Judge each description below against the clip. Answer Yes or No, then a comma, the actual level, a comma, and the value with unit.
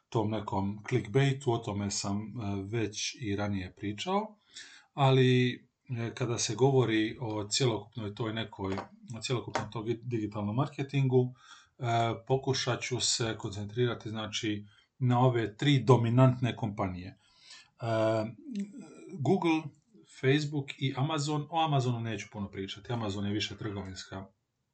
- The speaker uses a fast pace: No, slow, 110 wpm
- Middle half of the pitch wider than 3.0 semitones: Yes, average, 4.0 semitones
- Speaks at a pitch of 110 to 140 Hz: Yes, low, 115 Hz